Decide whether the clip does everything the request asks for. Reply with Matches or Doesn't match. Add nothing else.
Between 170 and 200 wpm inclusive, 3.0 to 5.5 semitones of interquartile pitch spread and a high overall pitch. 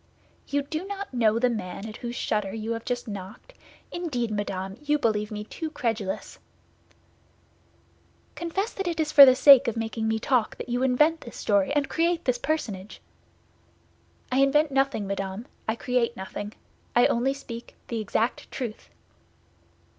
Doesn't match